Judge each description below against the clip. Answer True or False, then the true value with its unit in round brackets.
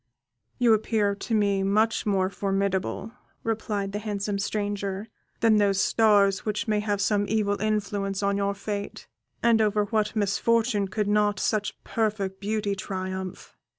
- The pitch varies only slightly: True (1.4 semitones)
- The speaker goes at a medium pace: True (145 wpm)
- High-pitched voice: True (205 Hz)